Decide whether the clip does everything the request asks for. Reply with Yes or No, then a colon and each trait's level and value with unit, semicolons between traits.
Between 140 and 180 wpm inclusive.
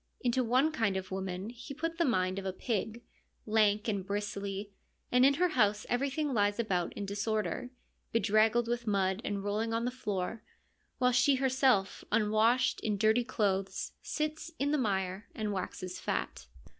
Yes: average, 165 wpm